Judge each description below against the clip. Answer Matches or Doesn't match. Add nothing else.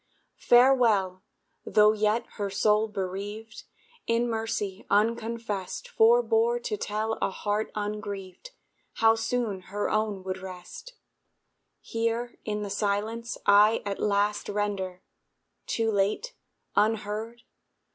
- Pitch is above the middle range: Matches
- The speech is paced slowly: Matches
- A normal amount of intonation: Doesn't match